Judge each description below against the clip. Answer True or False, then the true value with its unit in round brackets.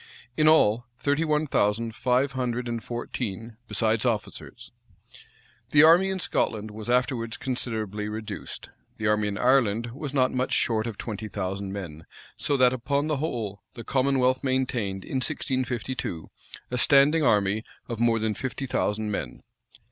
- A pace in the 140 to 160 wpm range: True (150 wpm)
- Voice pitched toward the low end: True (120 Hz)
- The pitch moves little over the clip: False (3.6 semitones)